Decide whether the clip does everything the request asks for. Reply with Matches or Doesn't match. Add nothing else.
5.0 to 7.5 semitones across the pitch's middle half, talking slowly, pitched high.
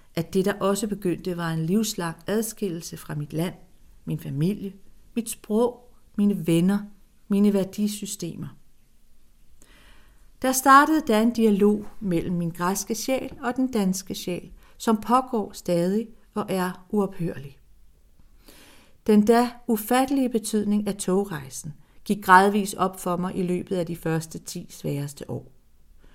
Doesn't match